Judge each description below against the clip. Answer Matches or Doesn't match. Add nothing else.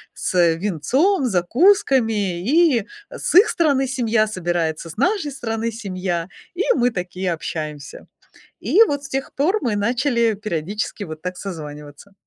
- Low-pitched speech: Doesn't match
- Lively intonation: Matches